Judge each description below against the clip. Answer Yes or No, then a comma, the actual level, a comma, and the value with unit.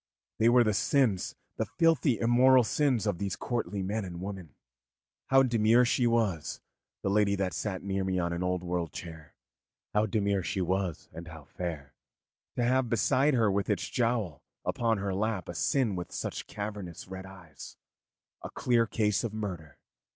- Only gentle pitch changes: No, average, 4.3 semitones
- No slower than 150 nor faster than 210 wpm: Yes, average, 175 wpm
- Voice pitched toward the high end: No, low, 100 Hz